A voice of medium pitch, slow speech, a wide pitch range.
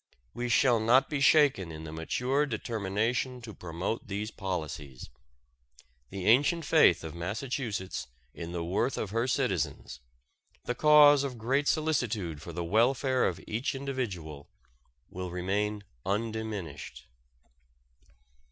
No: low, 110 Hz; slow, 125 wpm; wide, 6.4 semitones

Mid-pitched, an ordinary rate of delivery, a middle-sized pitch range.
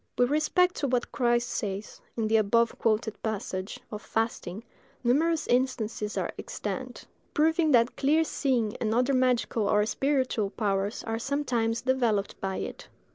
No: high, 235 Hz; average, 145 wpm; average, 3.4 semitones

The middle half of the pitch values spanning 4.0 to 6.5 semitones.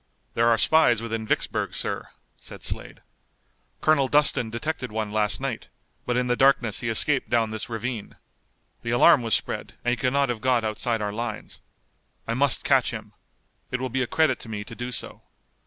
No: narrow, 2.6 semitones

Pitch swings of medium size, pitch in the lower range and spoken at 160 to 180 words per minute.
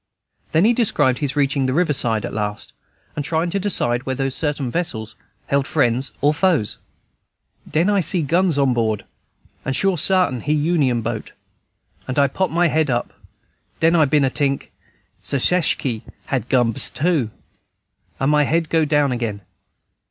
No: average, 4.5 semitones; medium, 145 Hz; average, 165 wpm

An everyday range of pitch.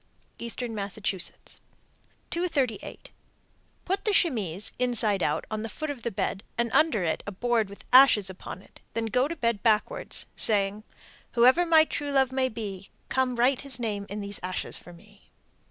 Yes: average, 4.5 semitones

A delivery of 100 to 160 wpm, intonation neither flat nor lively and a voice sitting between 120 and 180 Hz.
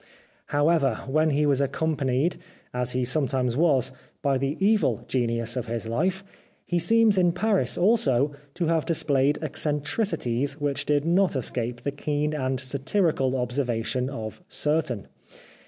Yes: average, 140 wpm; average, 4.1 semitones; medium, 140 Hz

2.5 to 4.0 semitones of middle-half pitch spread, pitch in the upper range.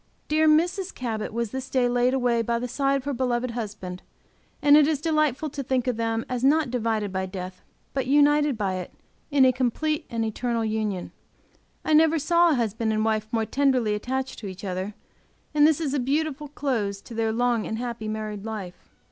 No: average, 4.6 semitones; high, 245 Hz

